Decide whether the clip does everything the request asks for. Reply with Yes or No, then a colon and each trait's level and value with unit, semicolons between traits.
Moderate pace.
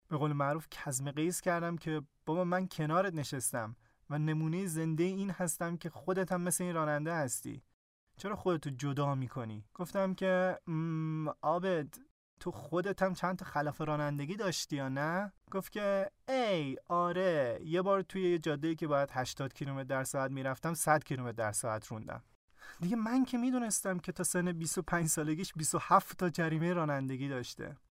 No: fast, 160 wpm